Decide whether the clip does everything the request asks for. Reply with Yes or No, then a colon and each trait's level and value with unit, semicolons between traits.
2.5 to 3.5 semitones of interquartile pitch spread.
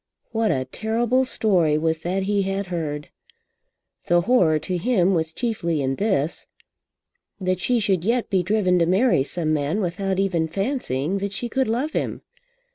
No: average, 5.1 semitones